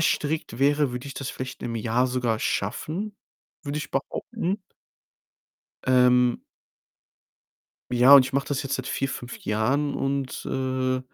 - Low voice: Yes, low, 130 Hz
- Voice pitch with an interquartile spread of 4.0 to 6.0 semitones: No, narrow, 2.4 semitones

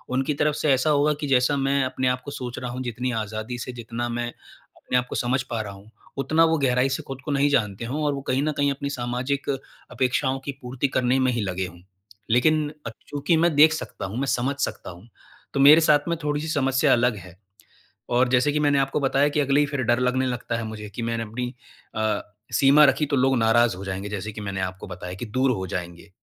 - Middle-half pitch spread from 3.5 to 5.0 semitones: Yes, average, 3.8 semitones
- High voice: No, low, 125 Hz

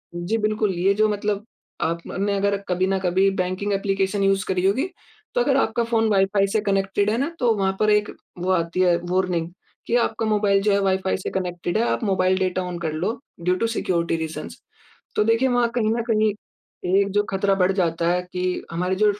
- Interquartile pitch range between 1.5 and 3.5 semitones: Yes, narrow, 2.5 semitones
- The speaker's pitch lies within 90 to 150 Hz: No, high, 195 Hz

